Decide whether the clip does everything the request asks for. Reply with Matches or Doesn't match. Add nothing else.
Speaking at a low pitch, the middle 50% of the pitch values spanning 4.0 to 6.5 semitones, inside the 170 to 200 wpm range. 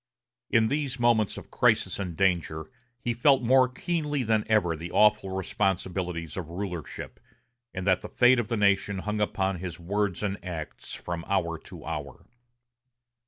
Doesn't match